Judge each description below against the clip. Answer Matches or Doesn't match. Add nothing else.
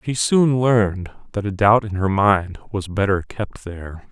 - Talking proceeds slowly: Doesn't match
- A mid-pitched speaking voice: Doesn't match